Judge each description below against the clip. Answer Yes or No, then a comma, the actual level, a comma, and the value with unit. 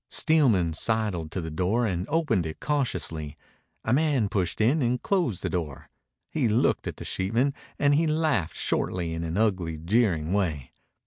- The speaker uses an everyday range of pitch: No, wide, 7.9 semitones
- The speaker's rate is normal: Yes, average, 170 wpm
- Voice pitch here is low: Yes, low, 105 Hz